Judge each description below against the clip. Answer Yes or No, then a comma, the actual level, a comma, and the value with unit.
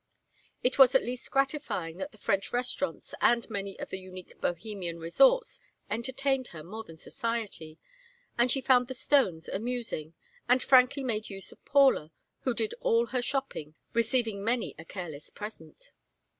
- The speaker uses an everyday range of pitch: No, wide, 5.7 semitones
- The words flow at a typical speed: Yes, average, 155 wpm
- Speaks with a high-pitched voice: Yes, high, 230 Hz